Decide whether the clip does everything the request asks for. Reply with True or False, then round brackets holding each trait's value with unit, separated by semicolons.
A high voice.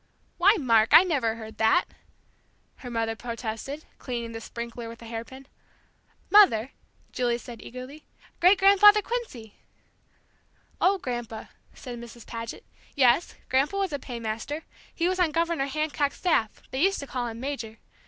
True (255 Hz)